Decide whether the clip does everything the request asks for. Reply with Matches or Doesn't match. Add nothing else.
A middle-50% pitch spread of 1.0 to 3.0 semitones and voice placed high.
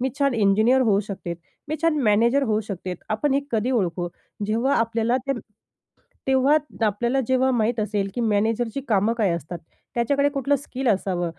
Doesn't match